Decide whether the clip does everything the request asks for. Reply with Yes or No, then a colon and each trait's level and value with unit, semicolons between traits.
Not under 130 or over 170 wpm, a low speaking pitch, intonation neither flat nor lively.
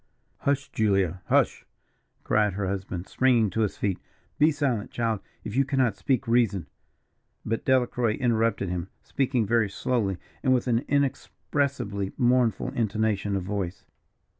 Yes: average, 140 wpm; low, 115 Hz; average, 4.3 semitones